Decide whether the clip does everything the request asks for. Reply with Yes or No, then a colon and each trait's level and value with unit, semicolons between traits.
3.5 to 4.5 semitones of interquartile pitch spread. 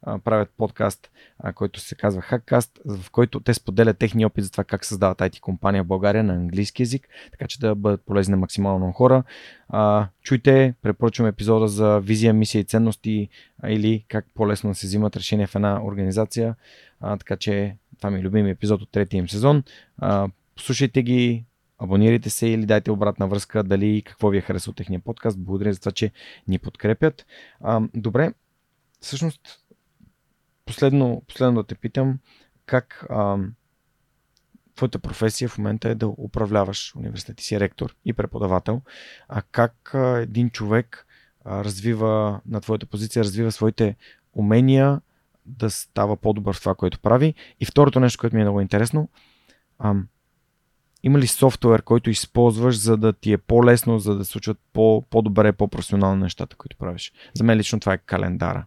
No: average, 2.8 semitones